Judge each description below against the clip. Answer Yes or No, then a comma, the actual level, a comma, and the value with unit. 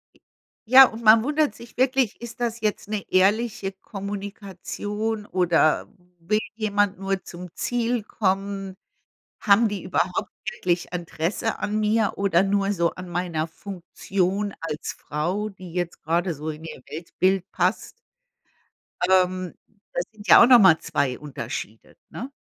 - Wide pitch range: No, average, 3.4 semitones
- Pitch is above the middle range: Yes, high, 195 Hz